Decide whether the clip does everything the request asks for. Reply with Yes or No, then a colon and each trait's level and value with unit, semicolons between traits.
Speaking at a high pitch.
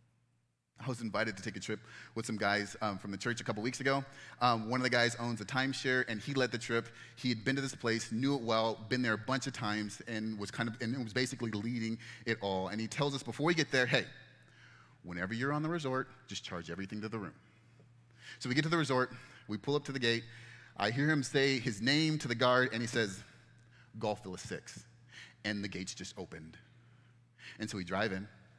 No: low, 120 Hz